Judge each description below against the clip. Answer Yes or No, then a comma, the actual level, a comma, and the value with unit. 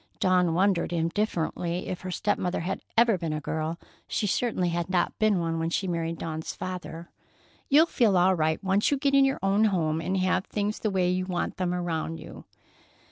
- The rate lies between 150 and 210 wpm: Yes, average, 200 wpm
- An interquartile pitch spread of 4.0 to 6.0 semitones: No, average, 3.2 semitones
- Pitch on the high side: No, medium, 180 Hz